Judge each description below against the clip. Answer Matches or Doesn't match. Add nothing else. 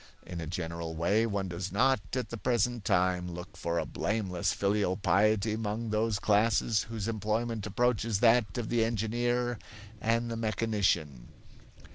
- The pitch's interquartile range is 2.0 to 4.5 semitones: Matches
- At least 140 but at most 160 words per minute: Matches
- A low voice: Matches